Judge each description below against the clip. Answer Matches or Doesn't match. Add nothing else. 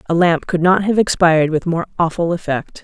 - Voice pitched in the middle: Matches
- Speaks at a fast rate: Matches